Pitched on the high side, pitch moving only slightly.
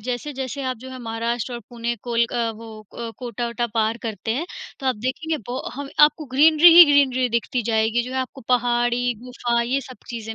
Yes: high, 245 Hz; narrow, 2.0 semitones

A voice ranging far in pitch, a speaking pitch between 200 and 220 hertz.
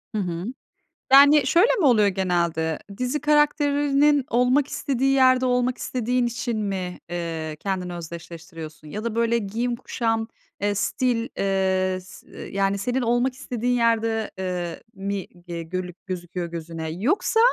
Yes: wide, 5.9 semitones; high, 215 Hz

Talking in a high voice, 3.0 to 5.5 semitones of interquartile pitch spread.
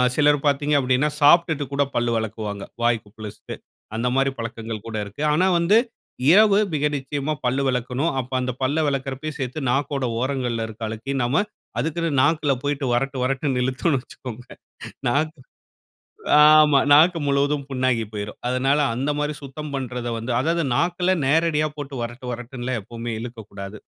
No: low, 135 Hz; average, 3.6 semitones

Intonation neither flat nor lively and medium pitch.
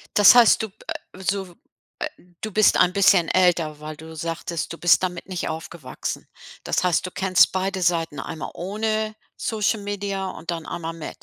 Yes: average, 3.3 semitones; medium, 180 Hz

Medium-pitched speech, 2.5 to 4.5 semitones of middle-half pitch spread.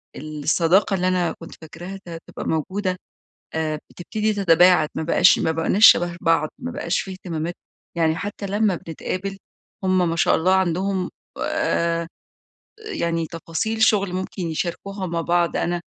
Yes: medium, 175 Hz; average, 2.8 semitones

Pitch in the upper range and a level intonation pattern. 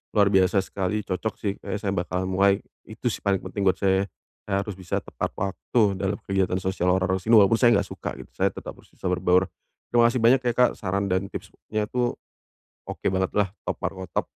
No: low, 100 Hz; narrow, 2.3 semitones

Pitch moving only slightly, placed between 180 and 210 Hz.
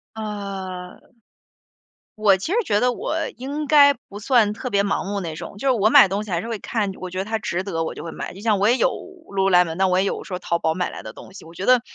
No: average, 3.6 semitones; high, 200 Hz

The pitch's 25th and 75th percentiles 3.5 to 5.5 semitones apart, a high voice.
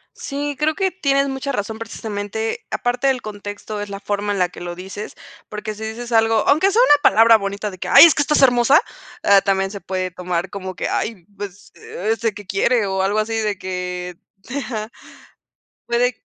Yes: average, 3.8 semitones; high, 215 Hz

